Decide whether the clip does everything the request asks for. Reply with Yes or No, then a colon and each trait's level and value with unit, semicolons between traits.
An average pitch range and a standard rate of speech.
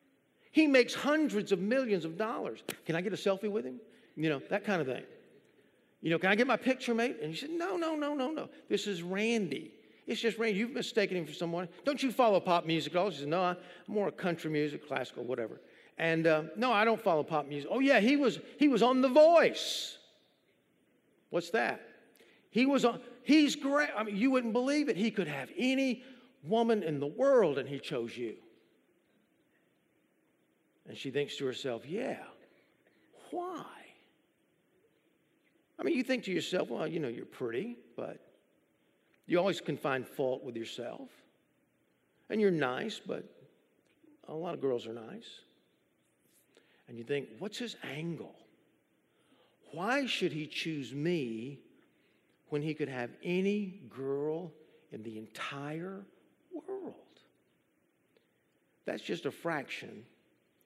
No: wide, 8.5 semitones; average, 165 wpm